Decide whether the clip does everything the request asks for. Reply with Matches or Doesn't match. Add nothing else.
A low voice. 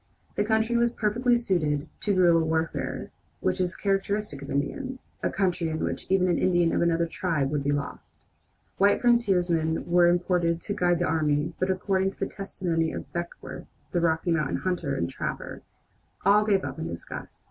Doesn't match